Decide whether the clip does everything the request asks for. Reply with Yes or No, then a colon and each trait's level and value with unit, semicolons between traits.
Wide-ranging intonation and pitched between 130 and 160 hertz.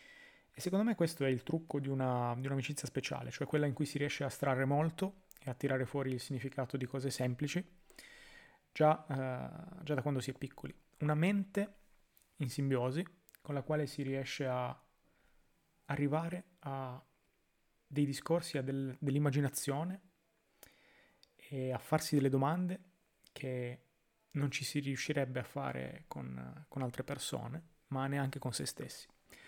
No: average, 3.5 semitones; medium, 140 Hz